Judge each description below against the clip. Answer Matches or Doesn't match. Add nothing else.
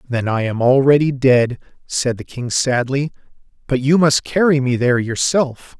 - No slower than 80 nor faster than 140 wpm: Doesn't match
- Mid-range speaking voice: Doesn't match